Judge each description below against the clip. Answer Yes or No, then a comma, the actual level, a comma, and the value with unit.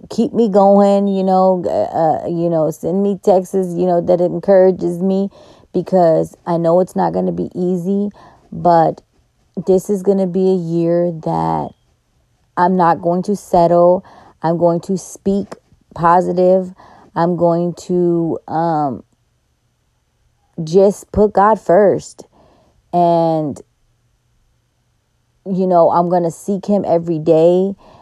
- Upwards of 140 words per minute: No, slow, 135 wpm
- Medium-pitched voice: Yes, medium, 175 Hz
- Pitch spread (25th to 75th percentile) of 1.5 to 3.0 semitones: Yes, narrow, 2.4 semitones